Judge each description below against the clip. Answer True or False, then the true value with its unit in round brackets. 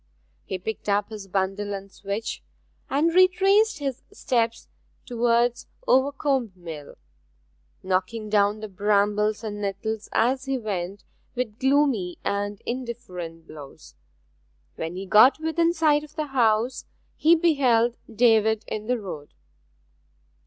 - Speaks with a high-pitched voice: True (220 Hz)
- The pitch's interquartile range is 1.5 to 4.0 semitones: False (4.9 semitones)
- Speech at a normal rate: False (125 wpm)